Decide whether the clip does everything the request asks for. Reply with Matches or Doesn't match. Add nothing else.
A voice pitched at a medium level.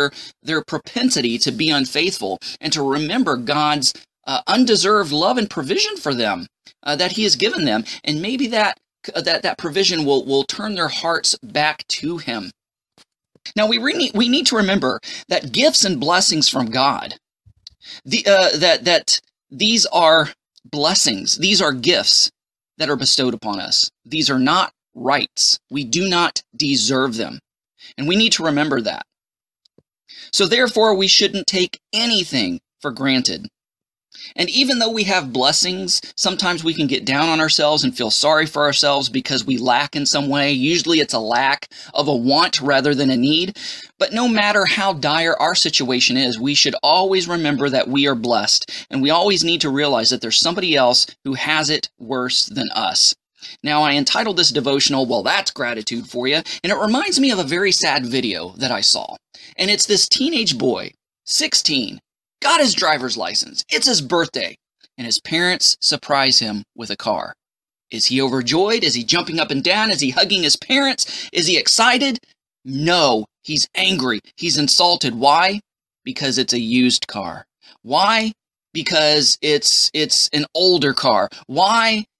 Matches